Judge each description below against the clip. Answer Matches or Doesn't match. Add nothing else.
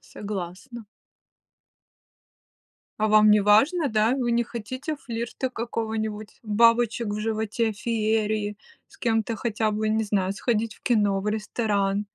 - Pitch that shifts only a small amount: Matches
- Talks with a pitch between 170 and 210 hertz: Doesn't match